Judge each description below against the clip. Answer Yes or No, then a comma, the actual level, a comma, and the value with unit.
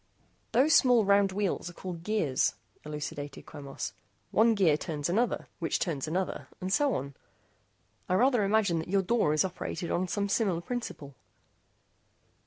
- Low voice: No, medium, 185 Hz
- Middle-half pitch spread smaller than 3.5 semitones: No, wide, 5.4 semitones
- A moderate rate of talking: Yes, average, 150 wpm